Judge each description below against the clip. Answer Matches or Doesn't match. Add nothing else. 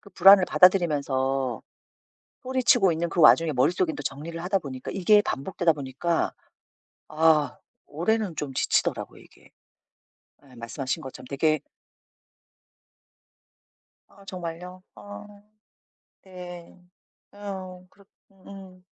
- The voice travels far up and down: Doesn't match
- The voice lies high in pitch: Doesn't match